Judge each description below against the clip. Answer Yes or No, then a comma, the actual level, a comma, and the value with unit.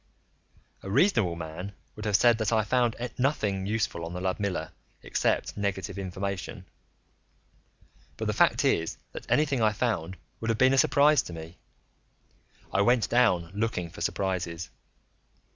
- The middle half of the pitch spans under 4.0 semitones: No, average, 4.4 semitones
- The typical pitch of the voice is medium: No, low, 100 Hz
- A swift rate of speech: No, average, 145 wpm